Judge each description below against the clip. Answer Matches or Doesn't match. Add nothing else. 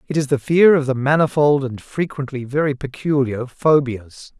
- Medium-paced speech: Matches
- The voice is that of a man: Matches